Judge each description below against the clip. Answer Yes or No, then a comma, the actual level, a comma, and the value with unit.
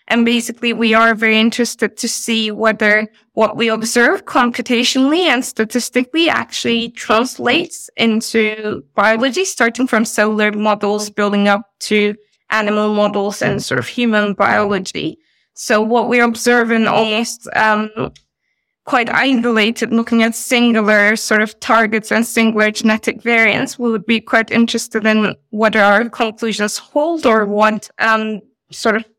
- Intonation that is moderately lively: No, narrow, 1.8 semitones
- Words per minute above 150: No, average, 140 wpm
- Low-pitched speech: No, high, 225 Hz